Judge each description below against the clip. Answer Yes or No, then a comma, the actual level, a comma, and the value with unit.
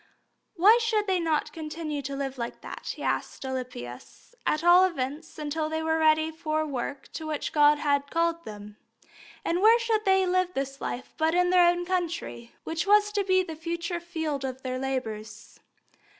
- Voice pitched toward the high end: Yes, very high, 320 Hz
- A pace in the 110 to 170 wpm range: No, average, 185 wpm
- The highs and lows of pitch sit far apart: No, average, 4.3 semitones